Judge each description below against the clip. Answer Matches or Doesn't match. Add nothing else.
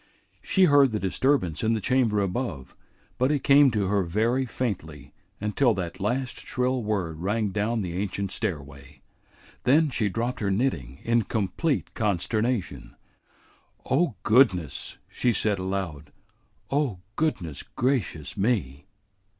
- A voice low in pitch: Matches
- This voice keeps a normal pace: Doesn't match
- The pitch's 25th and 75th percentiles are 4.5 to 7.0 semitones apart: Matches